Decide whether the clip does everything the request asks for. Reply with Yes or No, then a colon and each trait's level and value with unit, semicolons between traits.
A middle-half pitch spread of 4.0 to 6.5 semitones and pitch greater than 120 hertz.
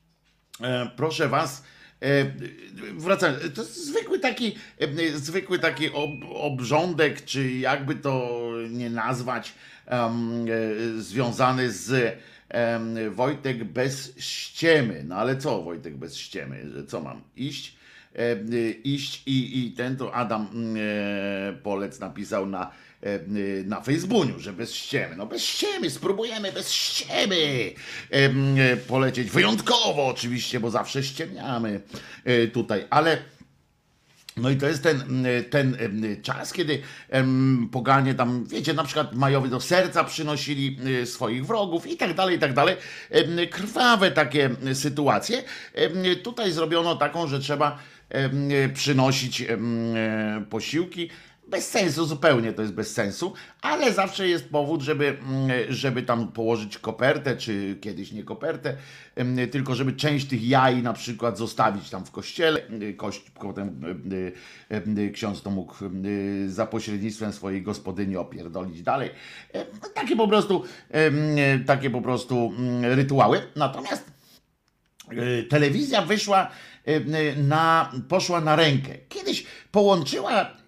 Yes: average, 5.3 semitones; low, 130 Hz